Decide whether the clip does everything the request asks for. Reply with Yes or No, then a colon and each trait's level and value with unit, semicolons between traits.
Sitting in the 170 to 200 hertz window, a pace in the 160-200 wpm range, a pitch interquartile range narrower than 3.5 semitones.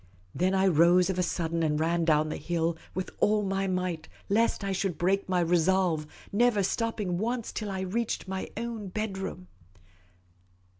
Yes: medium, 185 Hz; average, 165 wpm; average, 2.7 semitones